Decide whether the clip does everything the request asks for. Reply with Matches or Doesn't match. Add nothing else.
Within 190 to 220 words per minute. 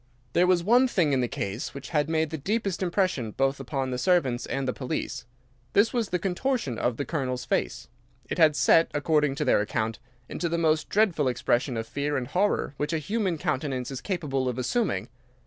Matches